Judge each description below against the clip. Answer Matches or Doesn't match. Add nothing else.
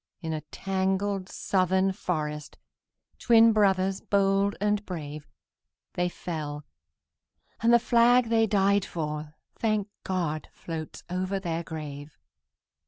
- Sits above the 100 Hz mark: Matches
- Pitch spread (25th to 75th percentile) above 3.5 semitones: Matches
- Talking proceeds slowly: Matches